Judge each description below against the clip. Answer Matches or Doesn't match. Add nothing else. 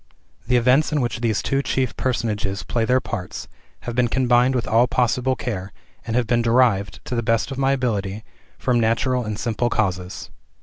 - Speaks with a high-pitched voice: Doesn't match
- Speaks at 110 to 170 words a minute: Doesn't match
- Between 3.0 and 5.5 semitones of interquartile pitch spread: Doesn't match